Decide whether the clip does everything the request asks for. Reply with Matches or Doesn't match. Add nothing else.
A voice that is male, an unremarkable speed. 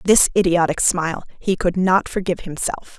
Doesn't match